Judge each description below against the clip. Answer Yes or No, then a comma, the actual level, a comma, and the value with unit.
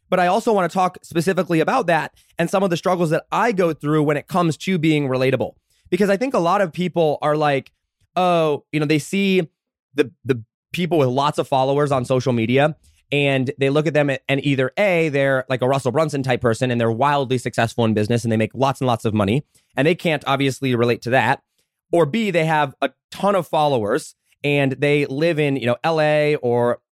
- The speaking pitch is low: No, medium, 145 Hz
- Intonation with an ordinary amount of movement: Yes, average, 4.3 semitones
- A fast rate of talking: Yes, fast, 225 wpm